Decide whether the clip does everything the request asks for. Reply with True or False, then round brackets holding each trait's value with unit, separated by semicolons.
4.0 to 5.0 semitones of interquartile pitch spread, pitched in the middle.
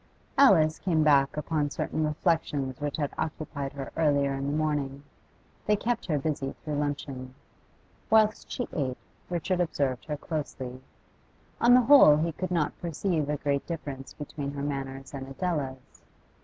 False (2.9 semitones; 150 Hz)